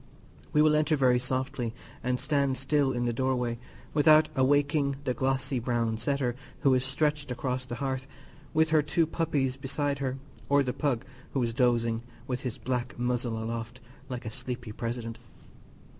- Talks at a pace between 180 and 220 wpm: No, average, 170 wpm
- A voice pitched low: Yes, low, 130 Hz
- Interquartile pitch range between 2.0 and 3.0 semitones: Yes, narrow, 2.6 semitones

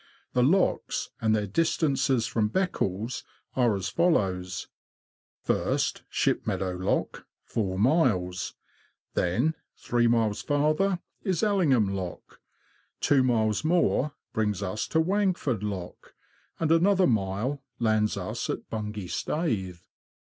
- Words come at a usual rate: No, slow, 120 wpm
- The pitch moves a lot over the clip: Yes, wide, 7.8 semitones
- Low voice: Yes, low, 115 Hz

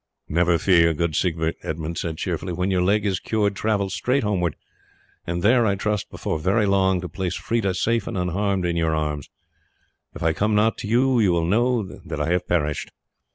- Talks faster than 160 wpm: Yes, average, 190 wpm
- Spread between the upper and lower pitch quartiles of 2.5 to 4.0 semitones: Yes, average, 3.7 semitones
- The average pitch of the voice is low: Yes, very low, 95 Hz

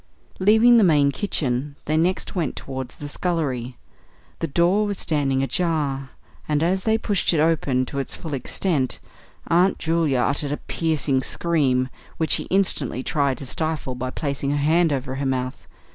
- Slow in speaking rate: No, average, 165 wpm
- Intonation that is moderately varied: Yes, average, 4.1 semitones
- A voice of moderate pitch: Yes, medium, 150 Hz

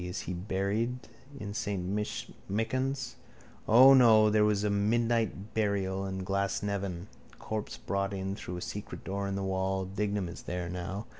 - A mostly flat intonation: Yes, narrow, 2.2 semitones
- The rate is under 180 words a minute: Yes, average, 155 wpm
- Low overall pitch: Yes, low, 100 Hz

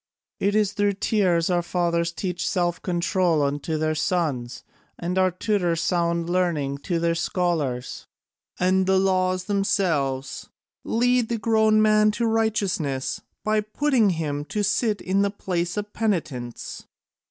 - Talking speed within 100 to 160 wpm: Yes, average, 140 wpm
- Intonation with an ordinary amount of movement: Yes, average, 3.7 semitones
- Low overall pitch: No, medium, 180 Hz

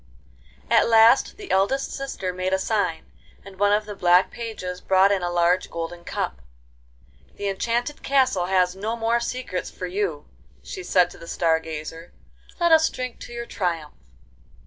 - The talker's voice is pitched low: No, high, 190 Hz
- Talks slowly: No, average, 170 wpm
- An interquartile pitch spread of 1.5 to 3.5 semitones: No, average, 4.8 semitones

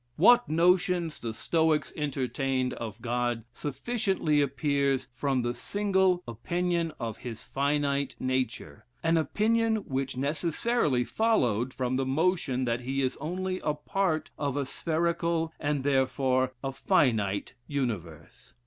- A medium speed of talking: No, slow, 125 wpm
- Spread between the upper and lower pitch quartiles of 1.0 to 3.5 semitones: No, average, 4.8 semitones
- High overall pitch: No, medium, 140 Hz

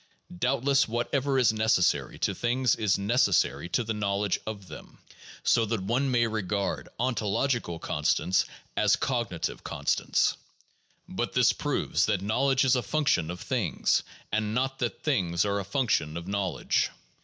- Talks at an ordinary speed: Yes, average, 150 wpm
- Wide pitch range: No, average, 4.5 semitones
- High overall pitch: No, low, 110 Hz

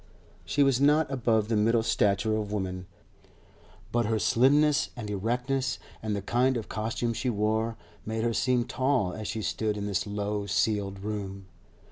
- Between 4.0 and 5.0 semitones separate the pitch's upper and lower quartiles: No, average, 3.1 semitones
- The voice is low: Yes, low, 110 Hz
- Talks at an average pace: Yes, average, 165 wpm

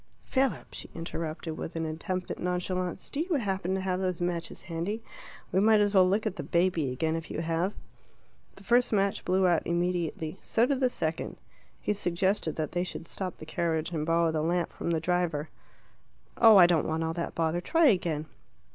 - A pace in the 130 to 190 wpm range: No, average, 200 wpm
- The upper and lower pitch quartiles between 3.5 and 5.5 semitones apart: No, average, 2.8 semitones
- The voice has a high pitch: No, medium, 175 Hz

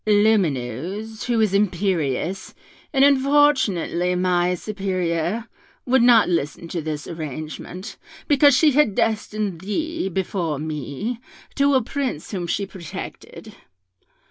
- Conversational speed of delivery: No, slow, 115 wpm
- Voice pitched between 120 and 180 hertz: No, high, 195 Hz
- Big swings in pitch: Yes, wide, 5.7 semitones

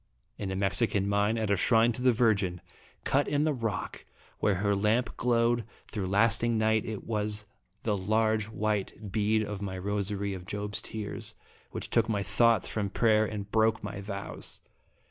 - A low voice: Yes, low, 105 Hz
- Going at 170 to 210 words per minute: Yes, average, 175 wpm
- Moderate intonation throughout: No, narrow, 1.9 semitones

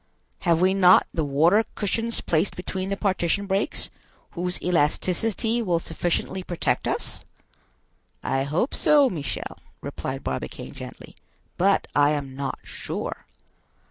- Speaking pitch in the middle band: Yes, medium, 180 Hz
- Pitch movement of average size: Yes, average, 3.6 semitones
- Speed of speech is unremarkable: No, slow, 125 wpm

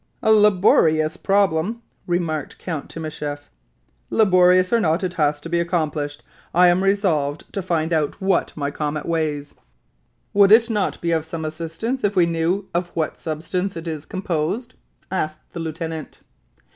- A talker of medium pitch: Yes, medium, 170 Hz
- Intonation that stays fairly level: No, average, 3.4 semitones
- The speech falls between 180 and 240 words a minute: No, average, 155 wpm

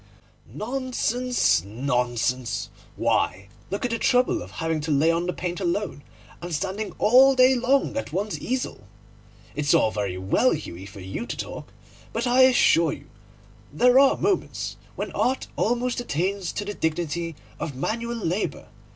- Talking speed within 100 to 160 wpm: Yes, average, 150 wpm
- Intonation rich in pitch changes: Yes, wide, 8.9 semitones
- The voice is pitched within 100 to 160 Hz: No, high, 190 Hz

